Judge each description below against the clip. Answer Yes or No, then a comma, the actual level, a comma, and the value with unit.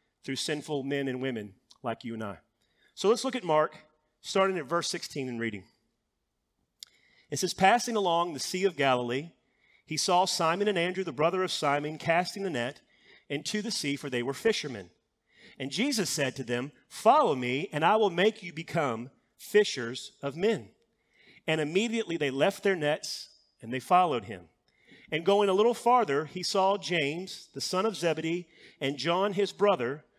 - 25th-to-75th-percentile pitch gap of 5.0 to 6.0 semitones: Yes, wide, 5.6 semitones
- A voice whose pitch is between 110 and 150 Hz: No, medium, 165 Hz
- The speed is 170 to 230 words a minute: Yes, average, 175 wpm